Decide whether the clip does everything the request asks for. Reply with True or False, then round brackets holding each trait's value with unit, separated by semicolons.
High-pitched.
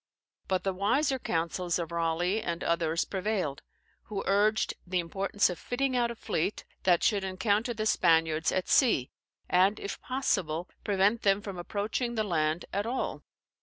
True (195 Hz)